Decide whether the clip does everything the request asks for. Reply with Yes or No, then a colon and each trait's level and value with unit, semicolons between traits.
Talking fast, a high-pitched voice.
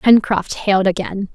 No: slow, 135 wpm; high, 200 Hz